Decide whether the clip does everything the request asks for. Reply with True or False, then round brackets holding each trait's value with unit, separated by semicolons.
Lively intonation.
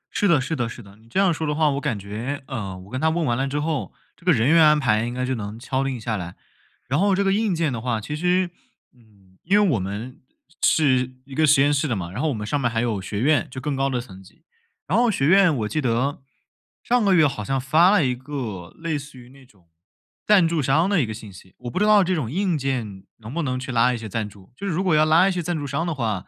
True (5.9 semitones)